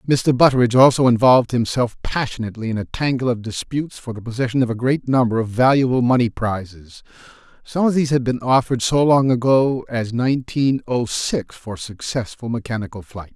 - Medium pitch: No, low, 125 Hz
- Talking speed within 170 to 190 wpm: Yes, average, 175 wpm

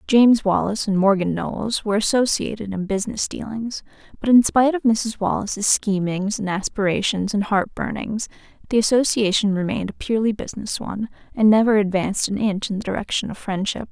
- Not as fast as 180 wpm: Yes, average, 170 wpm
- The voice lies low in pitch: No, high, 210 Hz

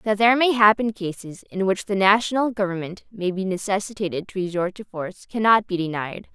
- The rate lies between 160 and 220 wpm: Yes, average, 190 wpm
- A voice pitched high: Yes, high, 200 Hz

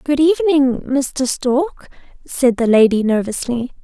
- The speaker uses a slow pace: Yes, slow, 125 wpm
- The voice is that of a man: No, female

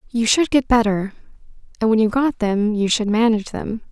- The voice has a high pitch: Yes, high, 225 Hz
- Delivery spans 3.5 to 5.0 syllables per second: No, 5.6 syllables/s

